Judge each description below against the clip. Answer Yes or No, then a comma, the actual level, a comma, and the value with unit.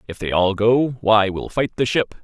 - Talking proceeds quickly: Yes, fast, 240 wpm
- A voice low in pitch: Yes, low, 110 Hz